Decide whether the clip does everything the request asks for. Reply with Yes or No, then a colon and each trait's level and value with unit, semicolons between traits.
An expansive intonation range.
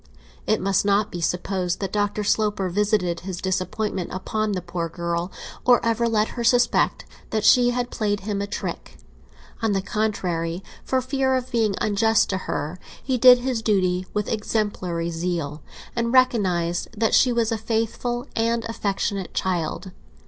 No: average, 3.8 semitones